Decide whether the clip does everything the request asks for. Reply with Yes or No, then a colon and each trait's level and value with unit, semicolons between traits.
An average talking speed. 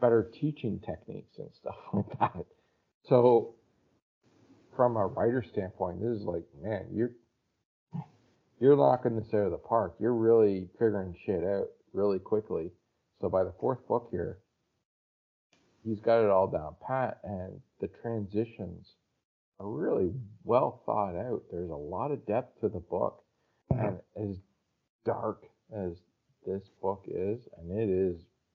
Yes: average, 145 wpm